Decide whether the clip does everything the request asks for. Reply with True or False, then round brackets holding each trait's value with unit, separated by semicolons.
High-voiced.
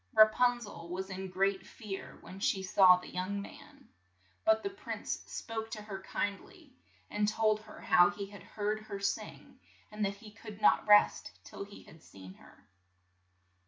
True (205 Hz)